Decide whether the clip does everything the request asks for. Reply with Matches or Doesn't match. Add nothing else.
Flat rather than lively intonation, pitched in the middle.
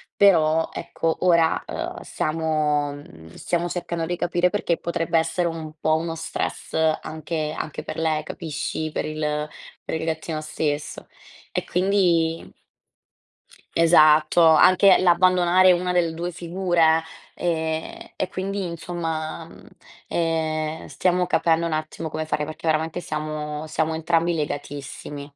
Matches